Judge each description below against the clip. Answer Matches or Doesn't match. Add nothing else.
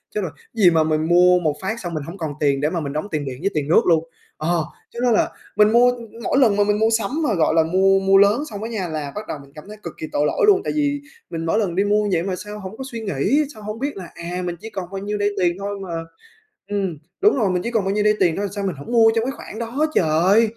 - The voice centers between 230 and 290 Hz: Doesn't match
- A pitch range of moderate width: Matches